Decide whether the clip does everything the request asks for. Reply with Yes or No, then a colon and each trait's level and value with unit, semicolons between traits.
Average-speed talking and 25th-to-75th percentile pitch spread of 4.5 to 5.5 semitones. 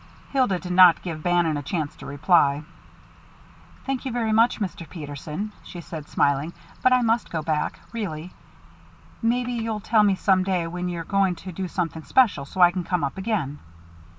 Yes: average, 180 wpm; average, 5.2 semitones